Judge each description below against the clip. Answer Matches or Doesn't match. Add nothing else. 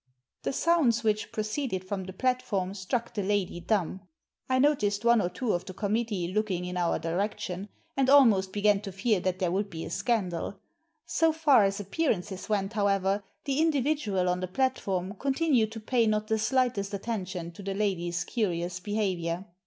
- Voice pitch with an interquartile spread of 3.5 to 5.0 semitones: Matches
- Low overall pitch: Doesn't match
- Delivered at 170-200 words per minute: Matches